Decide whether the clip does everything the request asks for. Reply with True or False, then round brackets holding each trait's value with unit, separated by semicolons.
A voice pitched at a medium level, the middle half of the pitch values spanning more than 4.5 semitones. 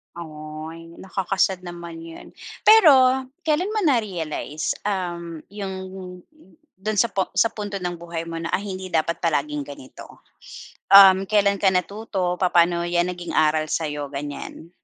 False (180 Hz; 3.4 semitones)